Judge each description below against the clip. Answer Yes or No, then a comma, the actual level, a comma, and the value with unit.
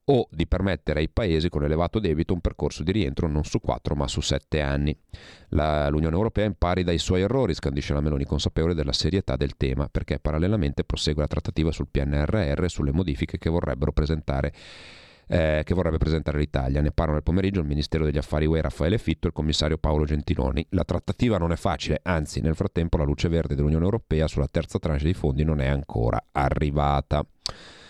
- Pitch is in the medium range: No, very low, 80 Hz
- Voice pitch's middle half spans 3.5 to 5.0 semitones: No, average, 3.0 semitones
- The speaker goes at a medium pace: No, fast, 190 wpm